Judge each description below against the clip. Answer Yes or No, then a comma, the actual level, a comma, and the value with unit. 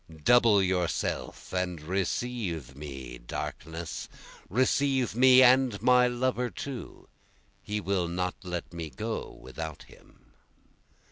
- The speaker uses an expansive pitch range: Yes, wide, 6.9 semitones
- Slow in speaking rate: Yes, slow, 110 wpm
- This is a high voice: No, very low, 95 Hz